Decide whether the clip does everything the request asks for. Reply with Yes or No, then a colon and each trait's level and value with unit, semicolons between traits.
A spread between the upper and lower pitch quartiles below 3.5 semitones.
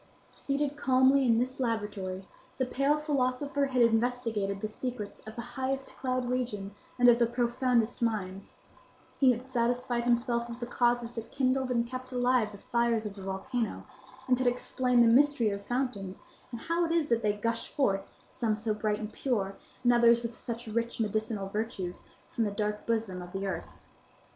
Yes: average, 3.0 semitones